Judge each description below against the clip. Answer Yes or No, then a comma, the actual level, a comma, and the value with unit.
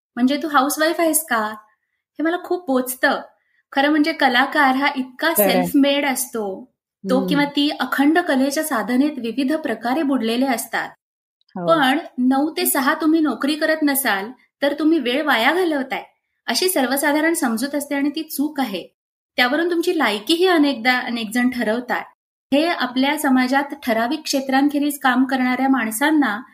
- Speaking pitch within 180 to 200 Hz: No, very high, 280 Hz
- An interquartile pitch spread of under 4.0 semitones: Yes, average, 3.2 semitones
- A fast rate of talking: Yes, fast, 145 wpm